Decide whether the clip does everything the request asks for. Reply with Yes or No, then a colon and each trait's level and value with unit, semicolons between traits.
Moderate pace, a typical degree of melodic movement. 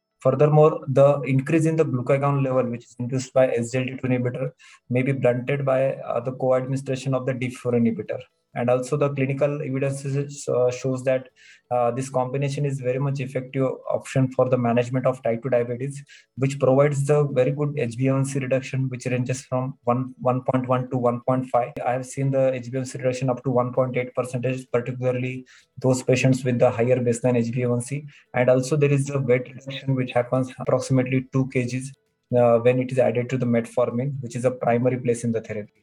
No: average, 180 wpm; narrow, 1.4 semitones